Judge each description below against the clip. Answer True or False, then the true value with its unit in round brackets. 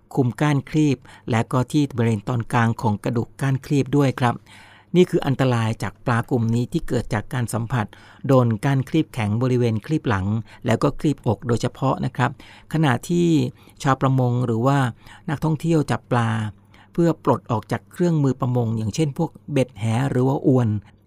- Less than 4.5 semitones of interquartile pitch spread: True (3.7 semitones)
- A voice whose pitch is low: True (125 Hz)